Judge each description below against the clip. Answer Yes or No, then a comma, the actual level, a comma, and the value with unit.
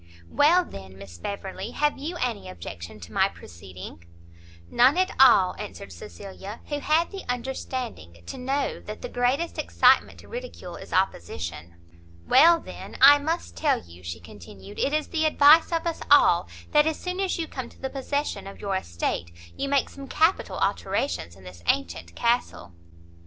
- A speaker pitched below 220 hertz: No, high, 245 Hz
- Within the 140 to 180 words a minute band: Yes, average, 170 wpm